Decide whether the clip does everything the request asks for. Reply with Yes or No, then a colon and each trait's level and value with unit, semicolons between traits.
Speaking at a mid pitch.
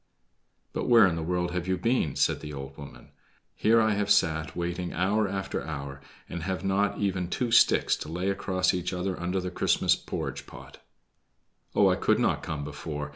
No: very low, 90 Hz